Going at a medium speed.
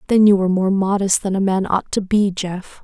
No: fast, 255 wpm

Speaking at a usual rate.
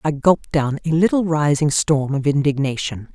Yes: average, 170 wpm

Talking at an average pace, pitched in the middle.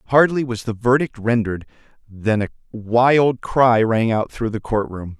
No: average, 160 wpm; low, 115 Hz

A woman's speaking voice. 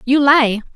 Yes: female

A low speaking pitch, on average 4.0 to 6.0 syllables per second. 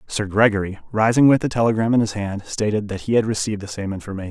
No: low, 105 Hz; 6.9 syllables/s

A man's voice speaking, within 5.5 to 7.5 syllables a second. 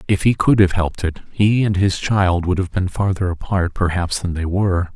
No: male; 5.2 syllables/s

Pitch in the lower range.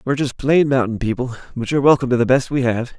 Yes: low, 125 Hz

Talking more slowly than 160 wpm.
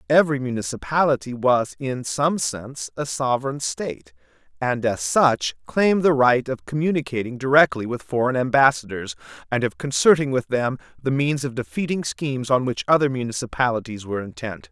Yes: average, 150 wpm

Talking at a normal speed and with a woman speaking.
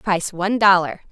Yes: average, 160 wpm; female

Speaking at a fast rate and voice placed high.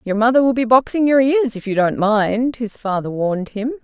Yes: fast, 235 wpm; high, 230 Hz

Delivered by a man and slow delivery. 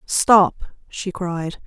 No: female; slow, 110 wpm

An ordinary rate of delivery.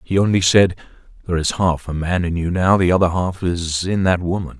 No: fast, 220 wpm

